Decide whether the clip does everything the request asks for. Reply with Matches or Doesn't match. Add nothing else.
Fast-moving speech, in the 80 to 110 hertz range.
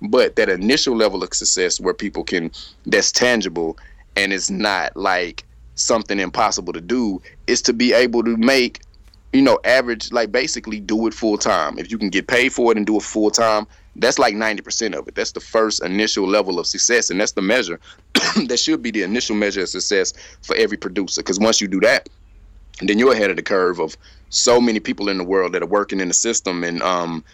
Matches